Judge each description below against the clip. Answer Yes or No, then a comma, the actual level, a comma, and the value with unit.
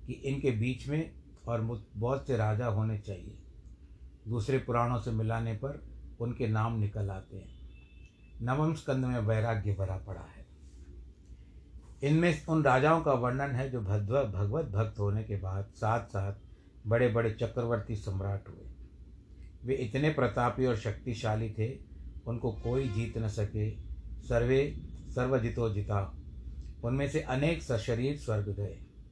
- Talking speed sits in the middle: Yes, average, 140 wpm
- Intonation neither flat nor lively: Yes, average, 4.5 semitones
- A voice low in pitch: Yes, low, 110 Hz